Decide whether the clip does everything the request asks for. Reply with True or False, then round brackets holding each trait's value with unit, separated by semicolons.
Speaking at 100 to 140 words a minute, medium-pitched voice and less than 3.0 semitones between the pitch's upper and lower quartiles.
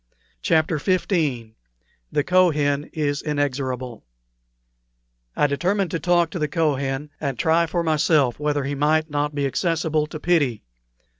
True (135 wpm; 150 Hz; 2.5 semitones)